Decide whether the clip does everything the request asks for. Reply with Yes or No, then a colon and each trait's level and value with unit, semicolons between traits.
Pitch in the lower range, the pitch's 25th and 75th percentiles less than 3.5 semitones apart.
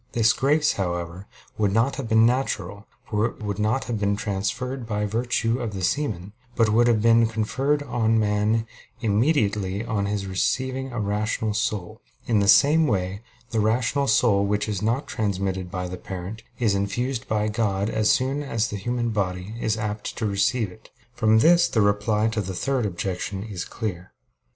Yes: low, 110 Hz; average, 2.9 semitones